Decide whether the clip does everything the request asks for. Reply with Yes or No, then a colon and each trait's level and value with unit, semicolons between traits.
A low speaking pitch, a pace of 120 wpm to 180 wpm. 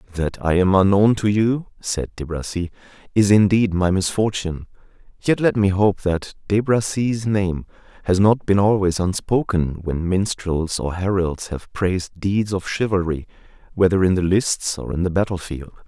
Yes: very low, 95 Hz; average, 165 wpm